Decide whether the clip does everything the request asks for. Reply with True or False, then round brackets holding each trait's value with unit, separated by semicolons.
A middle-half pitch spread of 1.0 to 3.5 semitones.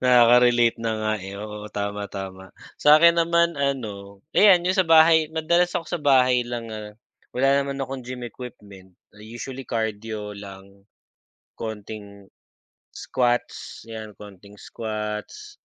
False (5.0 semitones)